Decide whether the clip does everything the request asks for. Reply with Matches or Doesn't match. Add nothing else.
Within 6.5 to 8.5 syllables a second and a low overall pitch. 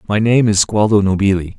Doesn't match